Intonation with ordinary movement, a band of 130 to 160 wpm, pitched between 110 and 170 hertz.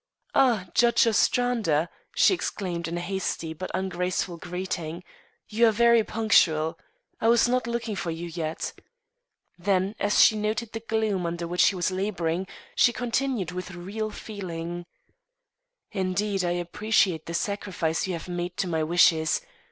No: average, 4.1 semitones; average, 150 wpm; medium, 185 Hz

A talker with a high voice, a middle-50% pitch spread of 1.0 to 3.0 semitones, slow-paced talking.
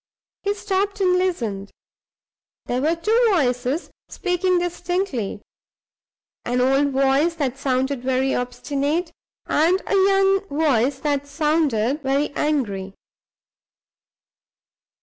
No: very high, 290 Hz; wide, 5.6 semitones; slow, 100 wpm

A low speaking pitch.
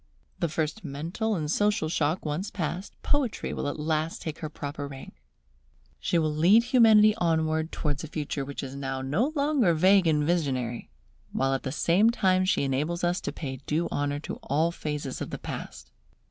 No: medium, 160 Hz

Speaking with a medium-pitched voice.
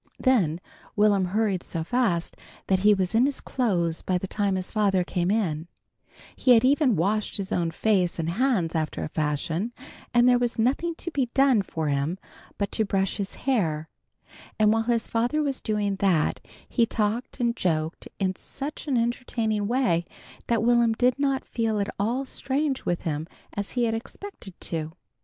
No: high, 210 Hz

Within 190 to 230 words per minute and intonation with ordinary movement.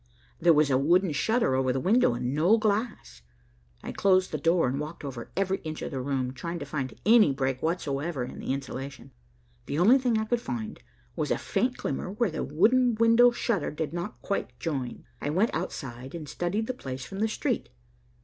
No: average, 200 wpm; wide, 7.9 semitones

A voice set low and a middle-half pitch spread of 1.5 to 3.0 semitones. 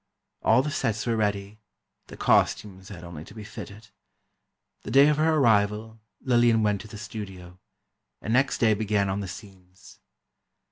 Yes: low, 105 Hz; narrow, 2.5 semitones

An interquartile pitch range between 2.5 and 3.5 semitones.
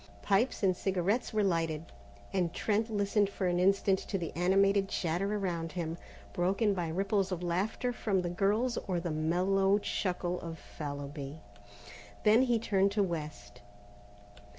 Yes: average, 3.0 semitones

